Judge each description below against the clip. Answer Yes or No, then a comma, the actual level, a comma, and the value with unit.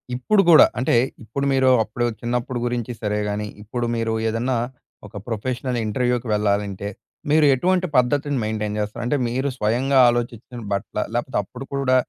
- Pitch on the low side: Yes, low, 120 Hz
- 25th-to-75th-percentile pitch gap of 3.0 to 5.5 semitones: Yes, average, 3.3 semitones